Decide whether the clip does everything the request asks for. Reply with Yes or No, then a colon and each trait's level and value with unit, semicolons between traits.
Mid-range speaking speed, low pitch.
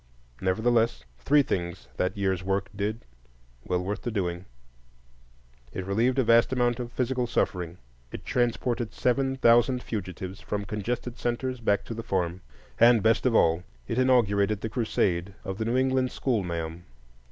Yes: average, 150 wpm; low, 110 Hz